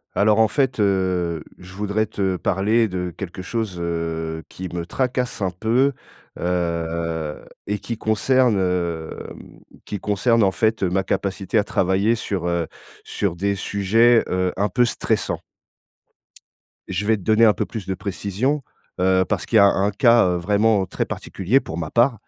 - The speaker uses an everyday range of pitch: Yes, average, 3.6 semitones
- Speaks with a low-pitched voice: Yes, low, 100 Hz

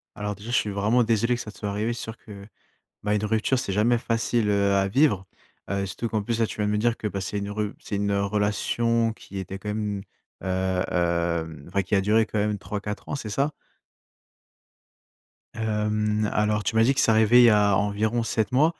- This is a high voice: No, low, 105 Hz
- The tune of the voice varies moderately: No, narrow, 2.0 semitones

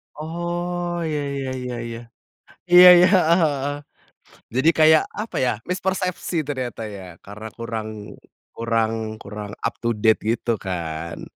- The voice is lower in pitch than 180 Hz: Yes, low, 135 Hz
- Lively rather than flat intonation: Yes, wide, 7.4 semitones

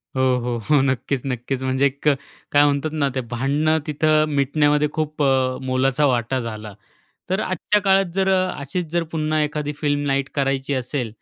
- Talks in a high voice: No, medium, 140 Hz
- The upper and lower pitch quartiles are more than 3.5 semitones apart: No, average, 2.7 semitones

